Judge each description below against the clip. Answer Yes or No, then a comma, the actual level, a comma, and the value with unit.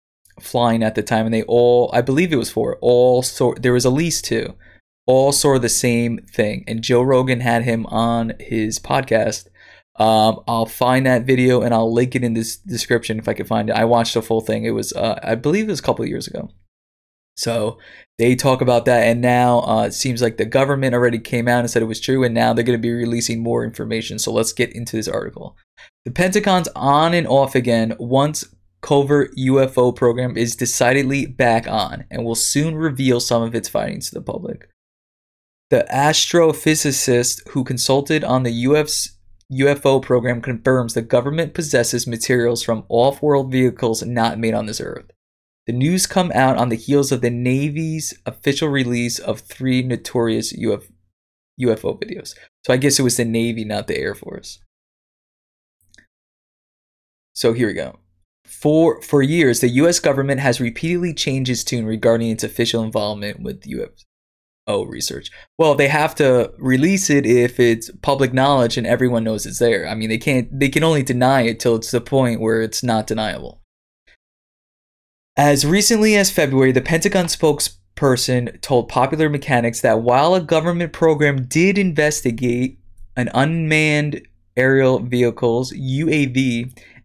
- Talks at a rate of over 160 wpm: Yes, average, 170 wpm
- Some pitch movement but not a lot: Yes, average, 3.2 semitones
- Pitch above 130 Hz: No, low, 120 Hz